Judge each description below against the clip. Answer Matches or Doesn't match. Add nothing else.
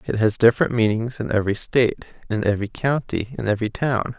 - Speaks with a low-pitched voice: Matches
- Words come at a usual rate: Matches